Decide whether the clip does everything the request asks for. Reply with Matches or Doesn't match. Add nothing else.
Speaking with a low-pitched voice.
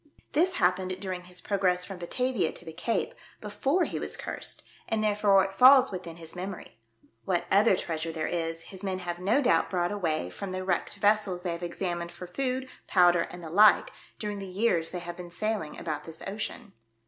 Doesn't match